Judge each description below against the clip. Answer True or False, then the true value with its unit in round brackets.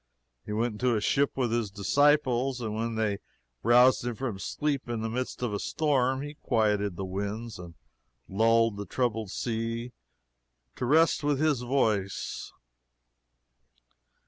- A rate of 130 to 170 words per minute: True (145 wpm)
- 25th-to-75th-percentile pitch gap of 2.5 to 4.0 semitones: True (3.6 semitones)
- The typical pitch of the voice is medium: False (115 Hz)